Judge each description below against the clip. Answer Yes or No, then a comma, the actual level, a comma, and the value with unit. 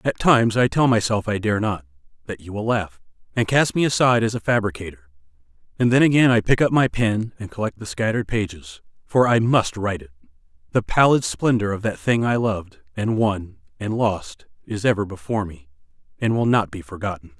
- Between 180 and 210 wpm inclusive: Yes, average, 195 wpm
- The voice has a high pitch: No, low, 110 Hz